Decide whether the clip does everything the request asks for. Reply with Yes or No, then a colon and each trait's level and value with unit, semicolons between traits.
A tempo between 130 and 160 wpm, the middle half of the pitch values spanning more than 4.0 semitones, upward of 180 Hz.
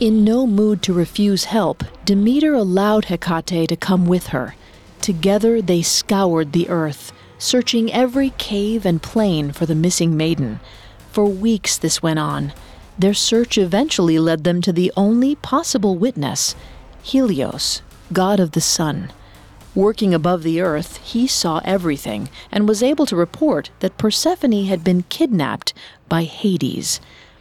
Yes: average, 145 wpm; average, 4.9 semitones; high, 190 Hz